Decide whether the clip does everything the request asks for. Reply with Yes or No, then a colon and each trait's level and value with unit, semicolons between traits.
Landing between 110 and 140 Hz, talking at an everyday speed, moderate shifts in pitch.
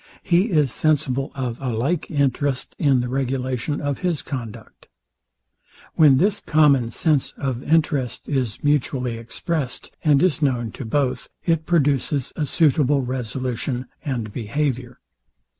No: low, 135 Hz; slow, 130 wpm; average, 3.0 semitones